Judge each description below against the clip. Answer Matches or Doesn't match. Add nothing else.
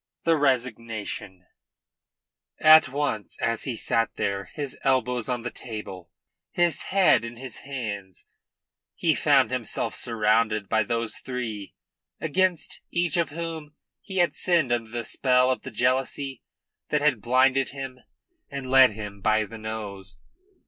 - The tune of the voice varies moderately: Matches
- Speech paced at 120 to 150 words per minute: Matches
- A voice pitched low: Matches